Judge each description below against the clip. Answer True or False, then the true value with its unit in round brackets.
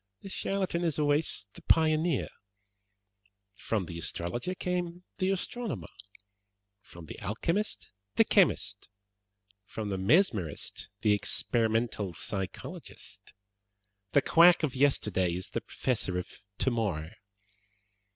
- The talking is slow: True (105 wpm)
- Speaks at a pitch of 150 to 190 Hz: False (120 Hz)